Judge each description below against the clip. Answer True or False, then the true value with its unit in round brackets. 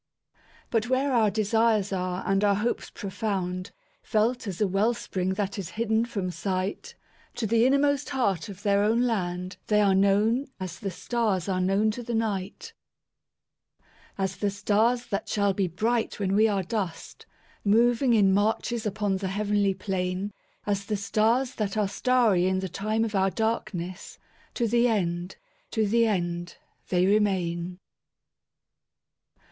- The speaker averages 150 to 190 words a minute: False (140 wpm)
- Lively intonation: False (2.9 semitones)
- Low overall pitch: False (205 Hz)